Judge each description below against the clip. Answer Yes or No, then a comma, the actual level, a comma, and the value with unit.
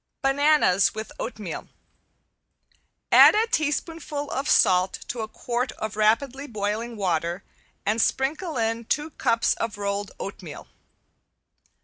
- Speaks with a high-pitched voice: Yes, high, 230 Hz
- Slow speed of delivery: Yes, slow, 115 wpm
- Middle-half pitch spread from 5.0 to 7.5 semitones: Yes, wide, 5.5 semitones